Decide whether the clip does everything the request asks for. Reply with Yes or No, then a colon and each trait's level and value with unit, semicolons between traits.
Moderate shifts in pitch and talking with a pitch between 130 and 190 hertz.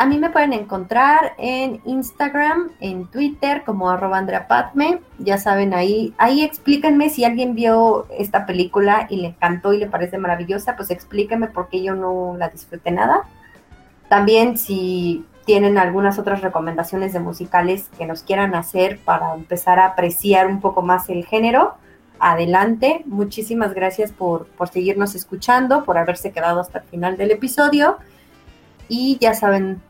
No: average, 4.5 semitones; high, 200 Hz